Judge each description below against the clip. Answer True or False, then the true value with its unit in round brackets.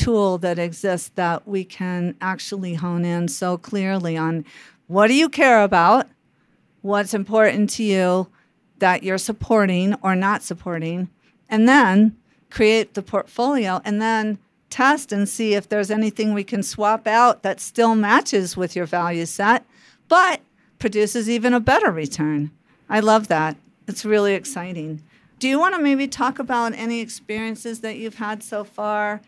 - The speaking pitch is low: False (210 Hz)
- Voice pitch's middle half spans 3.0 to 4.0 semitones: True (3.5 semitones)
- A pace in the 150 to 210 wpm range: True (160 wpm)